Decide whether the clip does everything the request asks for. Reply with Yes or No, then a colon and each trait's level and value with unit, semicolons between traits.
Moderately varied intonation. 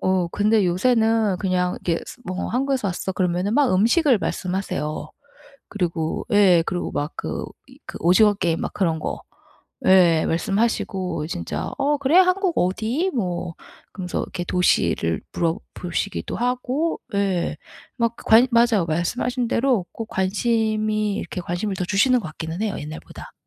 Yes: average, 4.8 semitones